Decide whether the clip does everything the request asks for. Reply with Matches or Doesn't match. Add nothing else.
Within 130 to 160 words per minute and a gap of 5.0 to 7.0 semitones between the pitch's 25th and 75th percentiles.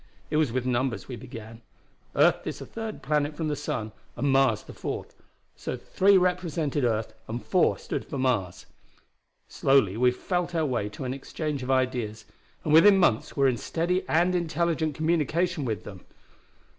Doesn't match